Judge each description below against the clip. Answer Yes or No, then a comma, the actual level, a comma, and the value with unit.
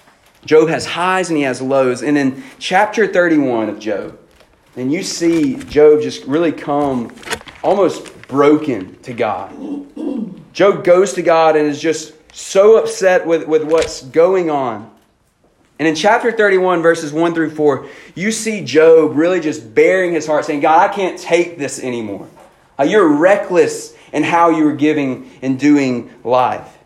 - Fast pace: No, average, 160 wpm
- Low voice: No, medium, 165 Hz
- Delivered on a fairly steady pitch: No, average, 5.0 semitones